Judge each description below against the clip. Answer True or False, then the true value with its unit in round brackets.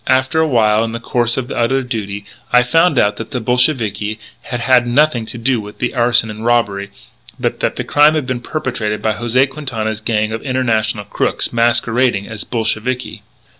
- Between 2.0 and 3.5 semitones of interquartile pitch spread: True (2.8 semitones)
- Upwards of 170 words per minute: True (185 wpm)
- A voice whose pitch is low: True (120 Hz)